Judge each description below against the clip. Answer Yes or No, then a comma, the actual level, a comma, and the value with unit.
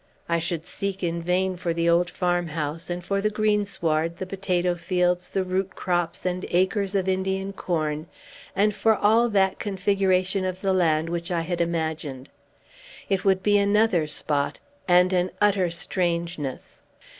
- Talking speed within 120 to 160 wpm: Yes, average, 155 wpm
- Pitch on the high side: No, medium, 180 Hz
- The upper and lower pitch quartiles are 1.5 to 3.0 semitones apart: Yes, narrow, 2.4 semitones